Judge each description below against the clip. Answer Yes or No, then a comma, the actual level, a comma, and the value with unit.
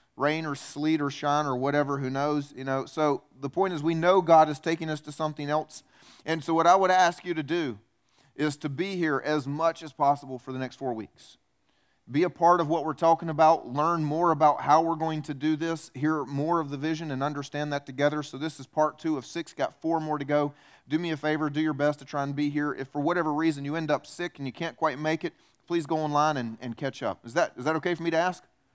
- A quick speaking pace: Yes, fast, 265 wpm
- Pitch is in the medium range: Yes, medium, 155 Hz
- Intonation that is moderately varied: No, narrow, 2.3 semitones